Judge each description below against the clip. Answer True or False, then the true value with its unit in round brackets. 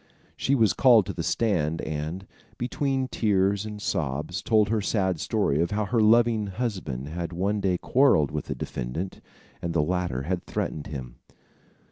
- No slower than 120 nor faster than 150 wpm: False (165 wpm)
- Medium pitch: False (95 Hz)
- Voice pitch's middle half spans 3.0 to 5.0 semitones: False (5.5 semitones)